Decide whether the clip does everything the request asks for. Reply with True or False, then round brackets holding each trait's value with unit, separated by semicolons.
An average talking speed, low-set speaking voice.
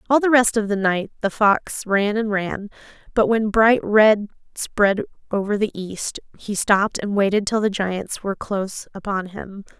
False (185 wpm; 205 Hz)